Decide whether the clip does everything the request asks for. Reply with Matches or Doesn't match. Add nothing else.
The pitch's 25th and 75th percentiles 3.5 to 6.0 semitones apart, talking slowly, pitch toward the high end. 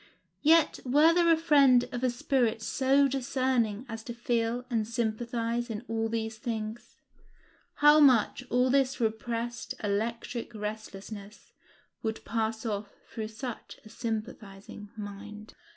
Doesn't match